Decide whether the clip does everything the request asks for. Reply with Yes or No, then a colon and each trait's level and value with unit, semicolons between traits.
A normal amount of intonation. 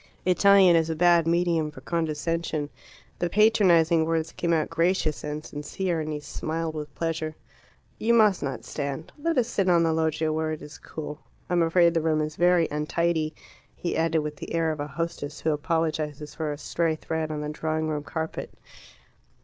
No: narrow, 1.7 semitones